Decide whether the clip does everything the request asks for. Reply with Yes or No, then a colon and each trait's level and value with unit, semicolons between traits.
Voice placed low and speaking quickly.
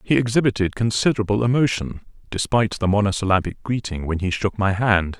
No: low, 105 Hz; average, 150 wpm